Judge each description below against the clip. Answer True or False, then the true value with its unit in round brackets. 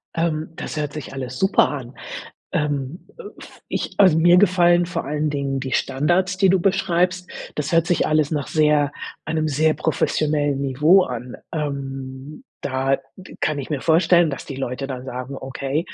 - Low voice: False (150 Hz)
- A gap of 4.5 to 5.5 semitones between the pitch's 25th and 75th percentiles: False (3.9 semitones)